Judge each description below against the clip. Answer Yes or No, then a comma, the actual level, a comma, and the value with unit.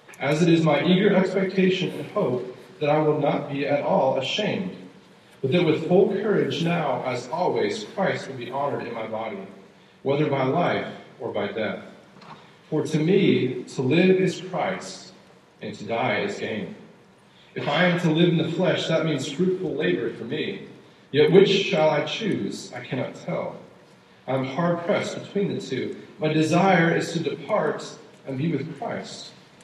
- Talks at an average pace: Yes, average, 175 wpm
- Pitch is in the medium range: Yes, medium, 160 Hz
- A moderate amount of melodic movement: Yes, average, 3.8 semitones